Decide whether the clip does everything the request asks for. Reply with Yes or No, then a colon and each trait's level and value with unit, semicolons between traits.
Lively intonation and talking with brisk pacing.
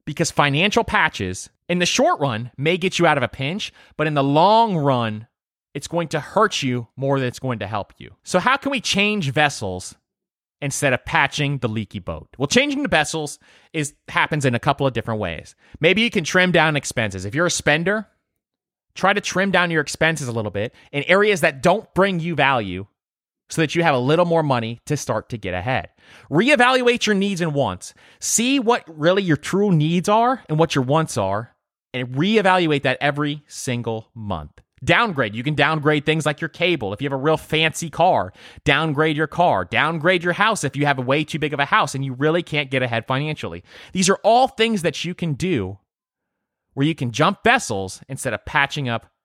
Yes: wide, 5.7 semitones; fast, 210 wpm